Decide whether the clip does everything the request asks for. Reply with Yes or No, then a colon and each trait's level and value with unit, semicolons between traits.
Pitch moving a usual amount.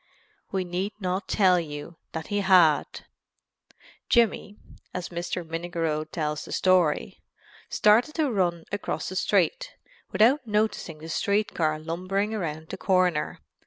Yes: average, 4.0 semitones